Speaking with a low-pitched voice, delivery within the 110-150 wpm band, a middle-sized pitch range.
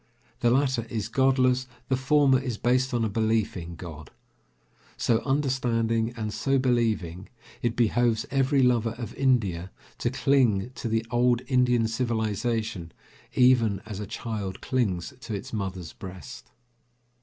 Yes: low, 115 Hz; average, 140 wpm; average, 3.3 semitones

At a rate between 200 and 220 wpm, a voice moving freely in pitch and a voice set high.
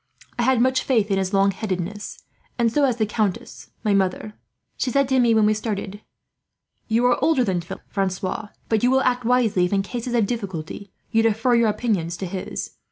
No: fast, 205 wpm; average, 3.7 semitones; high, 215 Hz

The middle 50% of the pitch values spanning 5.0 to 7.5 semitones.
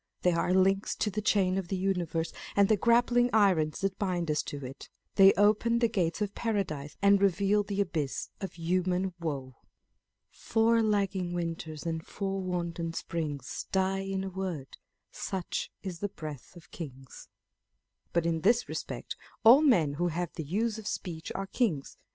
No: average, 3.5 semitones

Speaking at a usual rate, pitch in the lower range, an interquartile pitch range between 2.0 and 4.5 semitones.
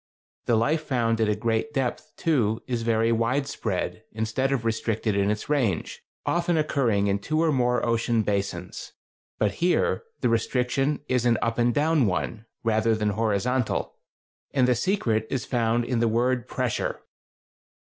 Yes: average, 160 wpm; low, 115 Hz; average, 3.0 semitones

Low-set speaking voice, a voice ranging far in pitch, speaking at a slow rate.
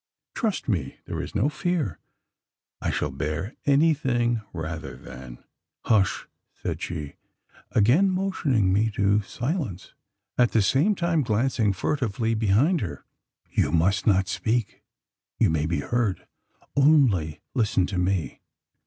Yes: low, 110 Hz; wide, 7.0 semitones; slow, 130 wpm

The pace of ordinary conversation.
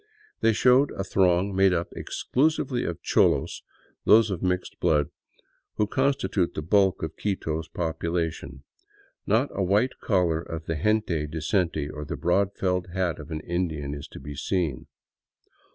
Yes: average, 150 wpm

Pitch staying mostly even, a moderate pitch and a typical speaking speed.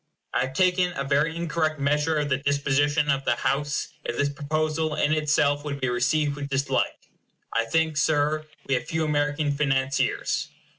Yes: narrow, 1.8 semitones; medium, 145 Hz; average, 170 wpm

